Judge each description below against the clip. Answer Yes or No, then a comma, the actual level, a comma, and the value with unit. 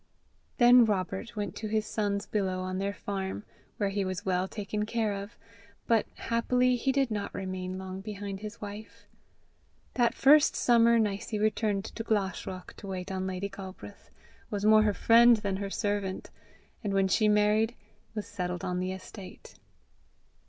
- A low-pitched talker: No, high, 205 Hz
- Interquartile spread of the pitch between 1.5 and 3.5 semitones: Yes, narrow, 2.4 semitones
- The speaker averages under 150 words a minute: No, average, 160 wpm